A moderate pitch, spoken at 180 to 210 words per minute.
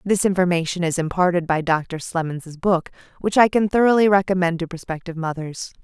No: medium, 175 Hz; average, 165 wpm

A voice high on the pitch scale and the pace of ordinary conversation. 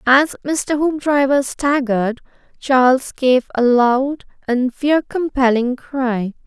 No: very high, 265 Hz; slow, 110 wpm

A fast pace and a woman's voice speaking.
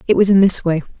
Yes: fast, 300 wpm; female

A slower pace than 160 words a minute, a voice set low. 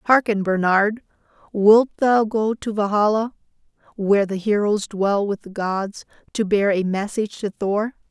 No: average, 150 wpm; high, 205 Hz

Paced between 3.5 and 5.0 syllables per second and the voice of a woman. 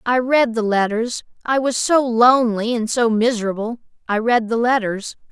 Yes: 4.8 syllables/s; female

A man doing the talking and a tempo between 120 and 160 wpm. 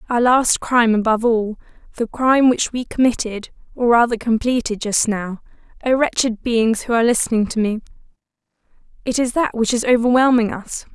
No: female; average, 155 wpm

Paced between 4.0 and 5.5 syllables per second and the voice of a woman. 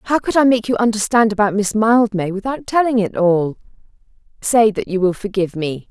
Yes: 5.4 syllables/s; female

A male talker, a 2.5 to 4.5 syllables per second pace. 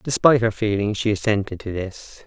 No: male; 5.4 syllables/s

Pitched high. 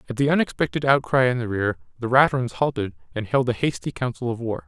No: low, 125 Hz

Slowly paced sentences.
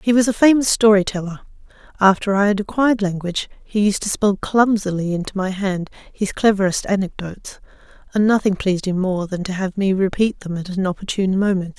No: average, 190 wpm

